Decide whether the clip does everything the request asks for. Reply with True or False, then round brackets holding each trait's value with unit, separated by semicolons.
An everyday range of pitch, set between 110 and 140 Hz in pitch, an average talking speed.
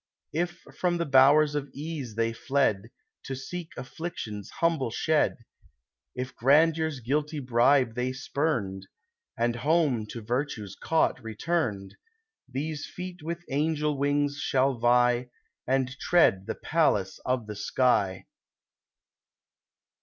False (4.9 semitones; 135 Hz; 120 wpm)